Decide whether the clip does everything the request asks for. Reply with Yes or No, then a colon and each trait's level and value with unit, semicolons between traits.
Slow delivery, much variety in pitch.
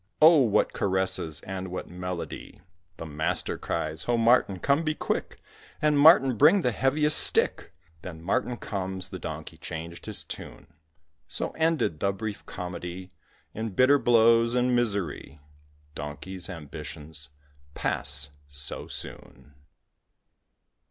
Yes: slow, 125 wpm; wide, 6.9 semitones